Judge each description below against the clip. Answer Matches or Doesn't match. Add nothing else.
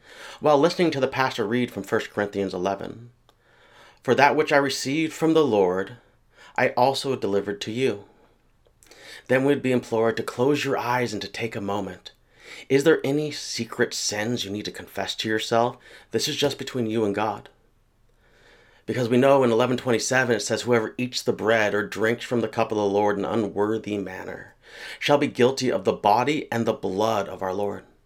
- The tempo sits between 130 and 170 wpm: Doesn't match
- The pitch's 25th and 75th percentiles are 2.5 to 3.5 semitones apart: Doesn't match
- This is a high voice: Doesn't match